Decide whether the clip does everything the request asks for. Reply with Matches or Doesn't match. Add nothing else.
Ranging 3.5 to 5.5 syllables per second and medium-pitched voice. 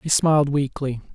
Matches